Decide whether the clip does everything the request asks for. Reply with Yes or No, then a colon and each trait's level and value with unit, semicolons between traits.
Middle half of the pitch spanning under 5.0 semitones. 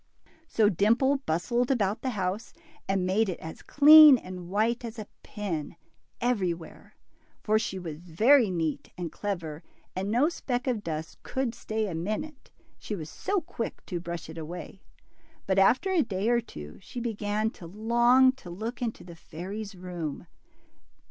No: average, 5.3 semitones